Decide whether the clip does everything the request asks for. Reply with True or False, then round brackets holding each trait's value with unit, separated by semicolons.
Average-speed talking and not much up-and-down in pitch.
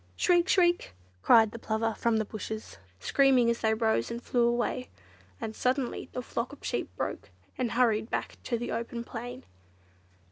True (170 wpm; 2.2 semitones)